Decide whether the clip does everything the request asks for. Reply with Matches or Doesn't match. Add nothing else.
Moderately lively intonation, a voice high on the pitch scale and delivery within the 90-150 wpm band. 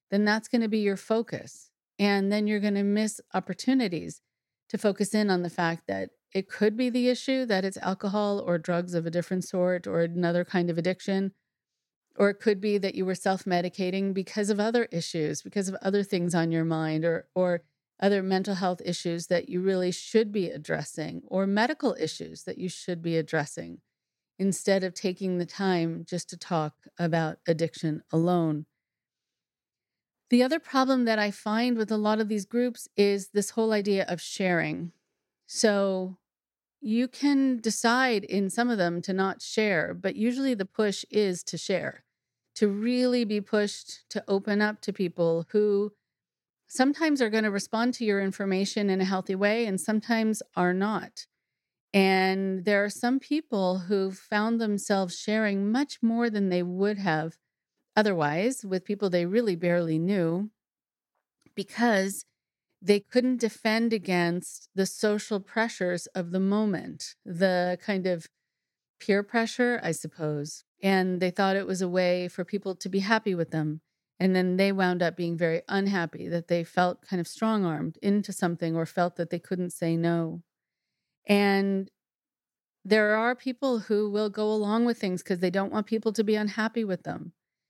Doesn't match